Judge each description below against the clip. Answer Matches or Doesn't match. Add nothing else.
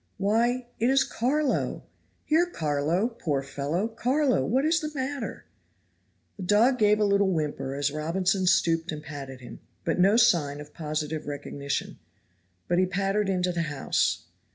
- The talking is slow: Doesn't match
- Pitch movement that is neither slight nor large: Doesn't match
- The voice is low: Doesn't match